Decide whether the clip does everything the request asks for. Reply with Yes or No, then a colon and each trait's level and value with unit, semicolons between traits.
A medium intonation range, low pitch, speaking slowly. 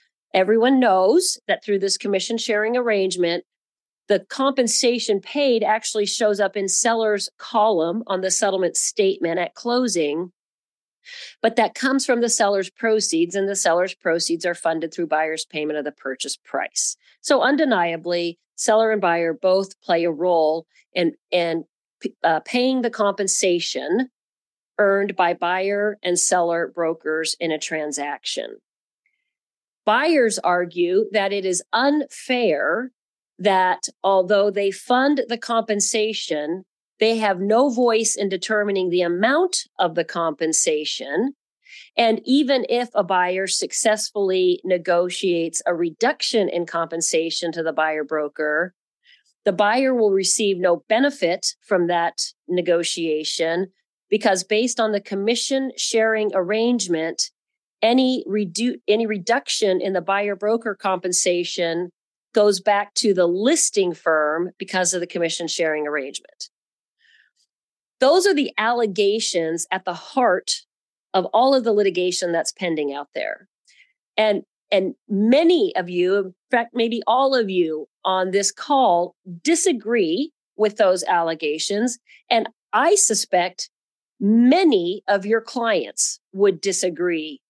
No: average, 4.8 semitones; high, 200 Hz; slow, 125 wpm